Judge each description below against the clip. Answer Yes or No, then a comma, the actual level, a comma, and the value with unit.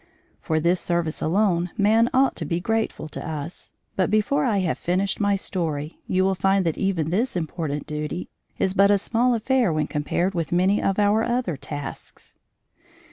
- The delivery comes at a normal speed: Yes, average, 180 wpm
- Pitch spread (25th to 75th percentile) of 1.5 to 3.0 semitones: No, average, 4.3 semitones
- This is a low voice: No, medium, 185 Hz